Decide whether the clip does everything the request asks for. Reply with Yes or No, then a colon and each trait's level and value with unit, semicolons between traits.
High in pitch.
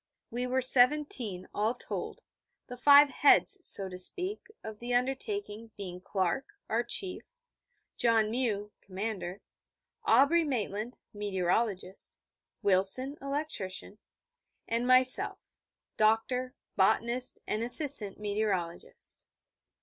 Yes: high, 230 Hz